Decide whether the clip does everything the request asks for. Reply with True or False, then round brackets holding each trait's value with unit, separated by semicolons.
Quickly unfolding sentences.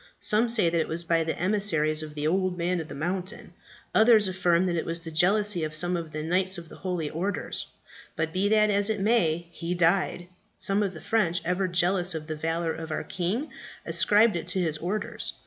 True (215 wpm)